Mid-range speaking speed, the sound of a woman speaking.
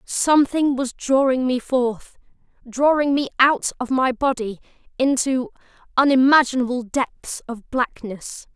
No: slow, 110 wpm; female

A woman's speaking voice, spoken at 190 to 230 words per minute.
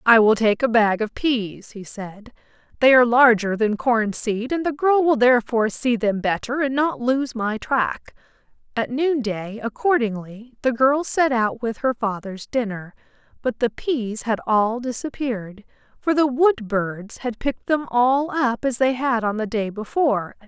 Yes: female; average, 195 wpm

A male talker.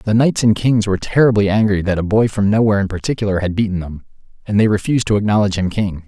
Yes: male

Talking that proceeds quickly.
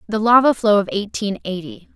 No: average, 185 wpm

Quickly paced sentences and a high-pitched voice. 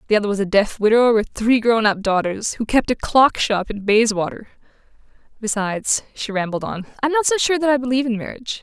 Yes: fast, 210 wpm; high, 225 Hz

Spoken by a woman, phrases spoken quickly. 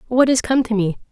Yes: female; fast, 270 wpm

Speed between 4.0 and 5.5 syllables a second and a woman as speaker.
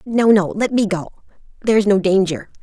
Yes: 5.4 syllables/s; female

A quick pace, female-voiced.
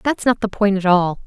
Yes: fast, 285 wpm; female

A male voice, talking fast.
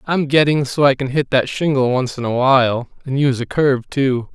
Yes: male; fast, 235 wpm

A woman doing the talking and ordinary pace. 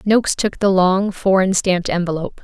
Yes: female; average, 170 wpm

